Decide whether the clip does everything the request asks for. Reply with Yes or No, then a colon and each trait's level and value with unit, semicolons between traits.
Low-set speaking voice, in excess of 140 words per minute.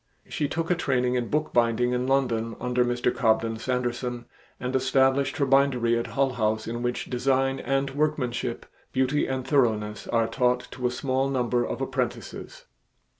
Yes: low, 125 Hz; average, 160 wpm